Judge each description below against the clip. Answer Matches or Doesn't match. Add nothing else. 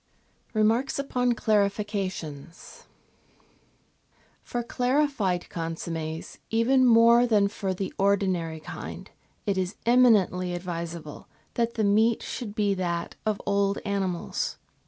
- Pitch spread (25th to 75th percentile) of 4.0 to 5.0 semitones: Matches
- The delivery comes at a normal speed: Doesn't match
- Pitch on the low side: Doesn't match